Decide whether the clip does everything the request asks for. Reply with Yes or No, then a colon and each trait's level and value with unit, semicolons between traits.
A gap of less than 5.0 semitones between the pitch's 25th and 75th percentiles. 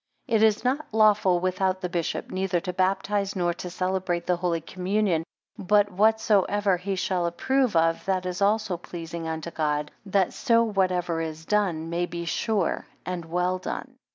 Yes: average, 2.9 semitones